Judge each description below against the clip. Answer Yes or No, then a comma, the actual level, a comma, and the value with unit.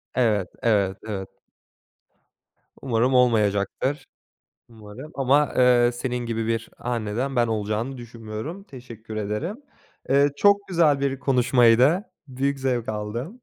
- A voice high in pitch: No, low, 120 Hz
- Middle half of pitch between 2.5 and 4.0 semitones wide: Yes, average, 3.7 semitones